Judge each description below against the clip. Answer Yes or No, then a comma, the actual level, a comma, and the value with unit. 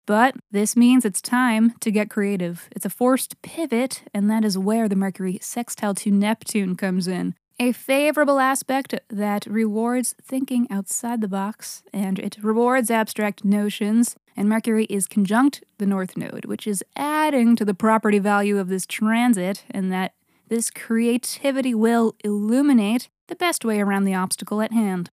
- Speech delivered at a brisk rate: No, average, 160 wpm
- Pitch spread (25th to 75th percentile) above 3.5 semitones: No, average, 3.1 semitones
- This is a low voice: No, high, 220 Hz